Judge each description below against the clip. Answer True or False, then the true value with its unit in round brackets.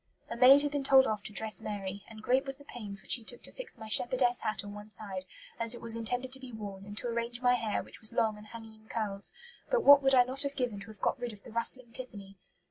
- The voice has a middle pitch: False (230 Hz)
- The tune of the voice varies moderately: True (3.3 semitones)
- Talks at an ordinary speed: False (280 wpm)